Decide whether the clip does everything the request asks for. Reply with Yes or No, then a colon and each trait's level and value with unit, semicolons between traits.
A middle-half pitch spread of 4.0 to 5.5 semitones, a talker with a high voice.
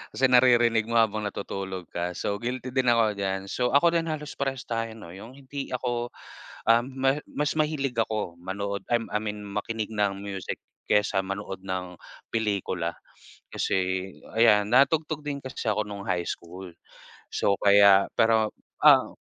No: average, 4.3 semitones; low, 110 Hz